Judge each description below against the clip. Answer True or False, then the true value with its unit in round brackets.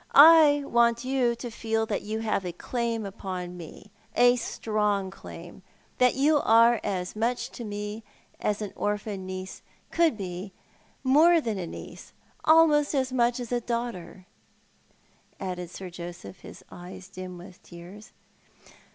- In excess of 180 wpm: False (155 wpm)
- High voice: True (215 Hz)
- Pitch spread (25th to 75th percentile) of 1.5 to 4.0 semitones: False (4.6 semitones)